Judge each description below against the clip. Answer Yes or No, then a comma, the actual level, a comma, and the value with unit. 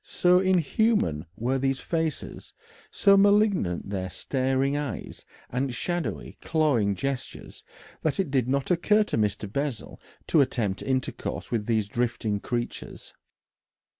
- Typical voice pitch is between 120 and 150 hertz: Yes, low, 135 Hz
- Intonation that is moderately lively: No, wide, 6.5 semitones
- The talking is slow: Yes, slow, 125 wpm